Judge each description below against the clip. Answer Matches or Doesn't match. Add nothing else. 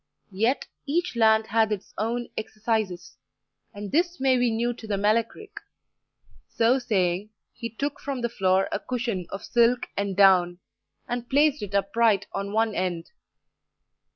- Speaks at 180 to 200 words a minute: Doesn't match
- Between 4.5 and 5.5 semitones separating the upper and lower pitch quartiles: Doesn't match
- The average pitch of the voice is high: Matches